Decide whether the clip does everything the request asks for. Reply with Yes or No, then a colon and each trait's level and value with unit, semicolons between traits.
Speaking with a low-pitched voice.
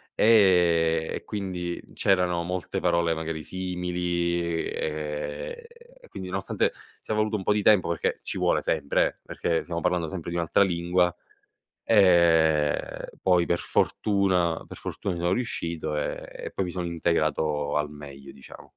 Yes: very low, 85 Hz